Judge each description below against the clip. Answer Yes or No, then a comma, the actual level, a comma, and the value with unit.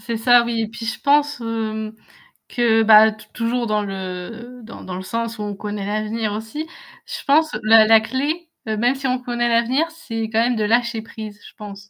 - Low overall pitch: No, high, 225 Hz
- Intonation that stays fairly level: Yes, narrow, 2.1 semitones